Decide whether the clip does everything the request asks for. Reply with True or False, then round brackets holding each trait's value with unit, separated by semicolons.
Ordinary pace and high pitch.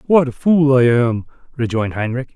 False (180 wpm; 130 Hz)